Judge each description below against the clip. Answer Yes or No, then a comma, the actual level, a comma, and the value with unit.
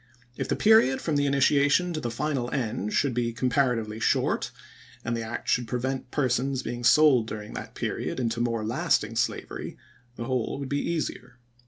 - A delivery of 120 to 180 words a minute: Yes, average, 175 wpm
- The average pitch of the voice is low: Yes, low, 125 Hz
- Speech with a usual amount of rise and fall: Yes, average, 3.1 semitones